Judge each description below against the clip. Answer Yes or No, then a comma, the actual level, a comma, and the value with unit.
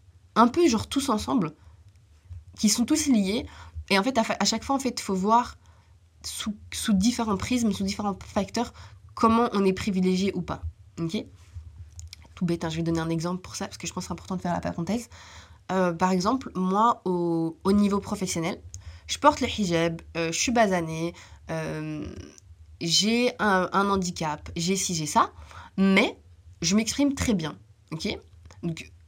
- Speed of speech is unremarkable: Yes, average, 185 wpm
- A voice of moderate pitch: Yes, medium, 180 Hz